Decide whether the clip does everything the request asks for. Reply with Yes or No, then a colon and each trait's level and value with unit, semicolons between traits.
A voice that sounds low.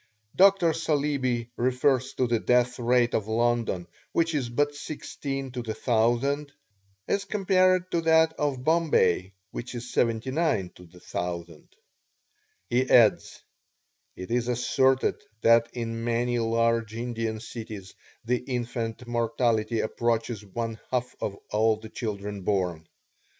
Yes: low, 120 Hz